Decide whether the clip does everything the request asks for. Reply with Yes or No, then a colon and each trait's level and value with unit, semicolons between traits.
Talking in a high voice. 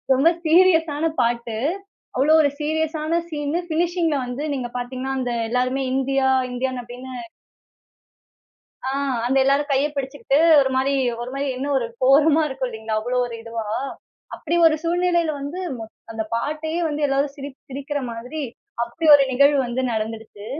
Yes: very high, 275 Hz